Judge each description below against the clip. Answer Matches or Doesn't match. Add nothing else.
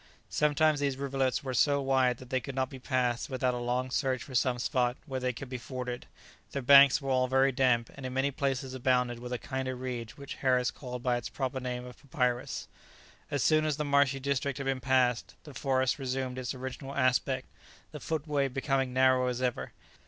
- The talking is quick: Matches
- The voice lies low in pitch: Matches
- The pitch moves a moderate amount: Doesn't match